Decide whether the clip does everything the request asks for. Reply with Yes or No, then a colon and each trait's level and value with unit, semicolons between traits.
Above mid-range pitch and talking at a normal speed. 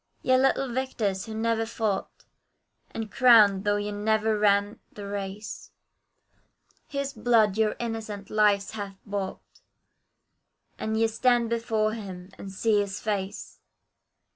No: high, 215 Hz; slow, 125 wpm